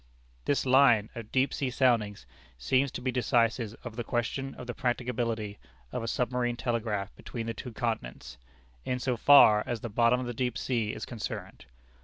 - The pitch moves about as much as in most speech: No, narrow, 2.3 semitones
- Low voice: Yes, low, 120 Hz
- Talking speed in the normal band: Yes, average, 180 wpm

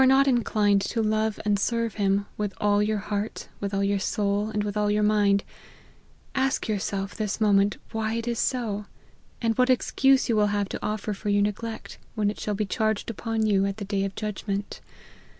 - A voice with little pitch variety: Yes, narrow, 1.6 semitones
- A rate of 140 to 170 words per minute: No, fast, 205 wpm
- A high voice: Yes, high, 210 Hz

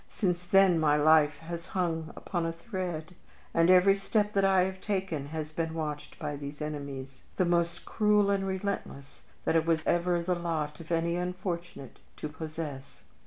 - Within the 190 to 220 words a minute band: No, average, 170 wpm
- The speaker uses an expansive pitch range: No, average, 3.1 semitones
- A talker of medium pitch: Yes, medium, 170 Hz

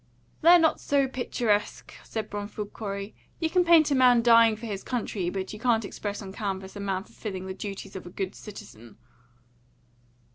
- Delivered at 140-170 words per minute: No, average, 180 wpm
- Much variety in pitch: No, average, 3.8 semitones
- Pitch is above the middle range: Yes, high, 210 Hz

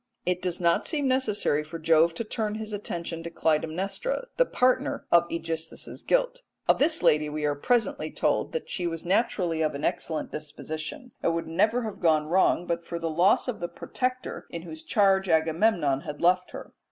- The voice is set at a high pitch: No, medium, 170 Hz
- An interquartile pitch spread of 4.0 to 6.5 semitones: Yes, average, 5.2 semitones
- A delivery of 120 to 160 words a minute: No, average, 190 wpm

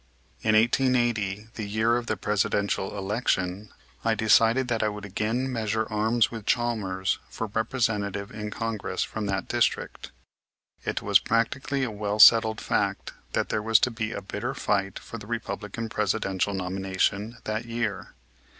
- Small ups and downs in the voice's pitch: Yes, narrow, 2.2 semitones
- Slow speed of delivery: No, average, 150 wpm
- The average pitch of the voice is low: Yes, low, 110 Hz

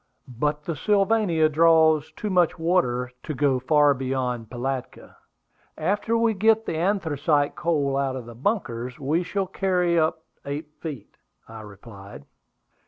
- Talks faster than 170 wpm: No, average, 140 wpm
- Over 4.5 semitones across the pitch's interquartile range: Yes, wide, 5.5 semitones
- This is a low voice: No, medium, 150 Hz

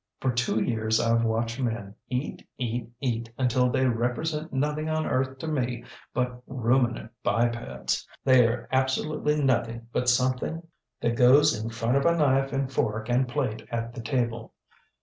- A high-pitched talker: No, low, 125 Hz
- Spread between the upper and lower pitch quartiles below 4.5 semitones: Yes, narrow, 2.4 semitones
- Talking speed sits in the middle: Yes, average, 155 wpm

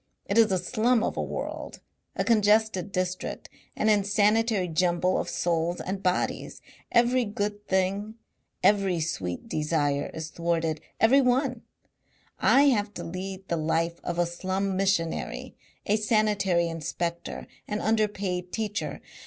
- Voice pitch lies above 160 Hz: Yes, high, 190 Hz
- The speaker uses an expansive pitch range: No, average, 3.8 semitones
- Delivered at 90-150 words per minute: Yes, slow, 135 wpm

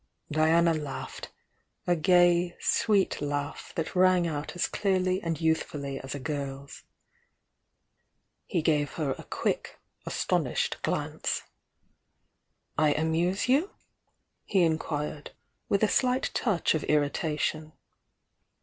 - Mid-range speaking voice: Yes, medium, 160 Hz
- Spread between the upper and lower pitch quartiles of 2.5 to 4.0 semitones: Yes, average, 3.5 semitones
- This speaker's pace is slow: Yes, slow, 115 wpm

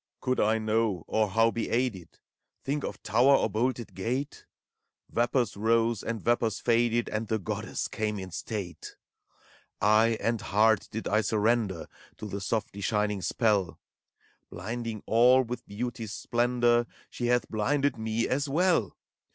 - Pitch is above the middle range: No, low, 115 Hz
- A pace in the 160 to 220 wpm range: No, average, 145 wpm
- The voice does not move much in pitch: Yes, narrow, 2.3 semitones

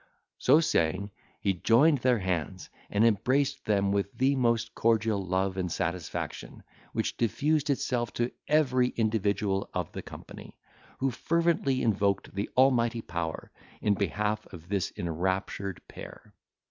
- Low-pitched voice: Yes, low, 105 Hz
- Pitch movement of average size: Yes, average, 4.6 semitones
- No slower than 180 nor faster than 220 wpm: No, slow, 135 wpm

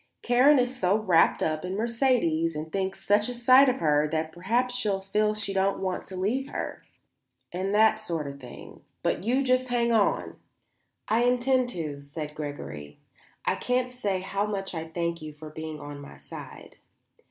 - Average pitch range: No, wide, 7.2 semitones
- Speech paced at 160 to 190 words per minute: Yes, average, 180 wpm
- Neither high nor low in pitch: No, high, 195 Hz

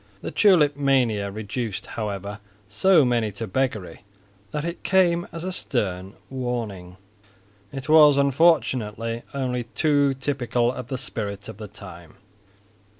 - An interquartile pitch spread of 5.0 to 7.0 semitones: Yes, wide, 5.5 semitones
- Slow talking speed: Yes, slow, 130 wpm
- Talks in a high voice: No, low, 125 Hz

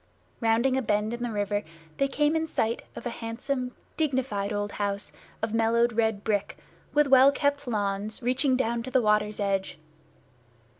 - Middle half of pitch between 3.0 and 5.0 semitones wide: Yes, average, 3.9 semitones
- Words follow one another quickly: No, average, 165 wpm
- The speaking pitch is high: Yes, high, 230 Hz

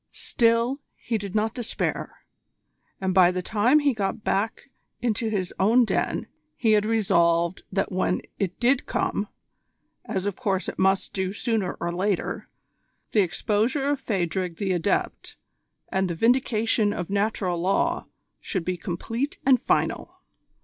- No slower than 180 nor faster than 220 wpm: No, average, 145 wpm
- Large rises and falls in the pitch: No, average, 3.7 semitones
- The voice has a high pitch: Yes, high, 205 Hz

